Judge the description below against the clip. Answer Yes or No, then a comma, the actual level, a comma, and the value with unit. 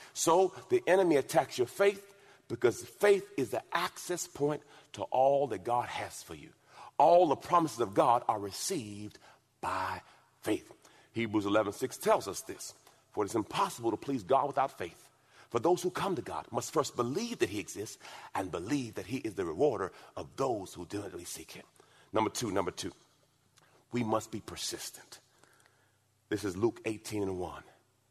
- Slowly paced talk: No, average, 175 wpm